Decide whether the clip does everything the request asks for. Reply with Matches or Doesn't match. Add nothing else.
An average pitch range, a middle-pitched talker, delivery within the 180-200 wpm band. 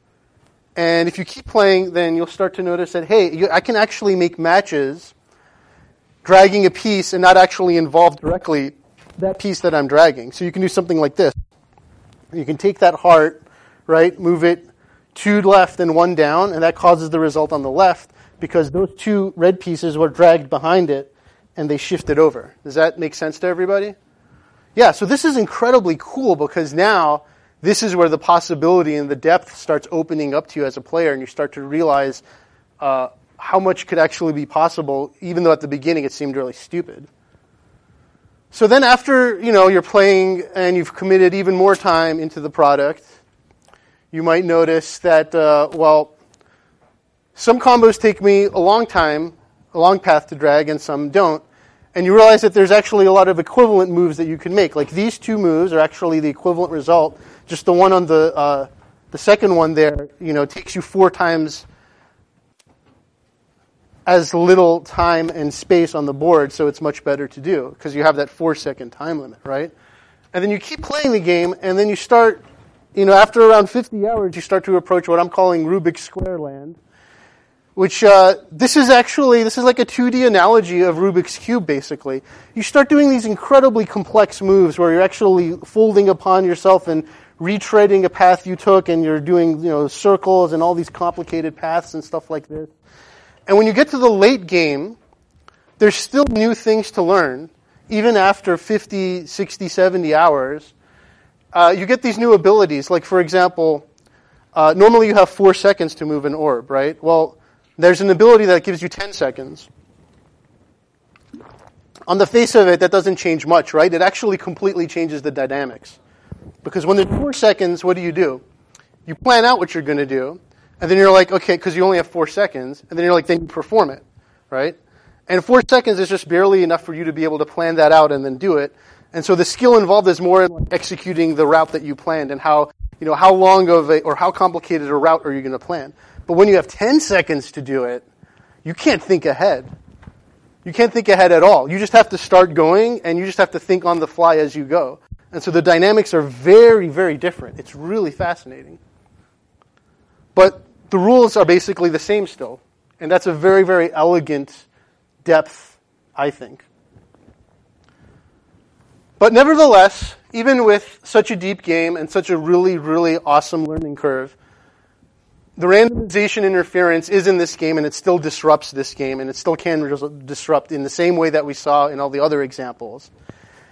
Matches